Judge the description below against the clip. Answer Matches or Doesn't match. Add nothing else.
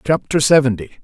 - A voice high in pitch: Doesn't match